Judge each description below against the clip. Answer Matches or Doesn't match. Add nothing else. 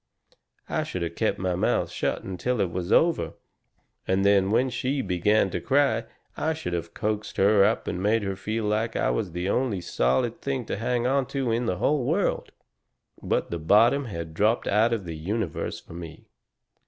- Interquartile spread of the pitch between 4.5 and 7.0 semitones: Matches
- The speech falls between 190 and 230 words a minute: Matches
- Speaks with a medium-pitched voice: Doesn't match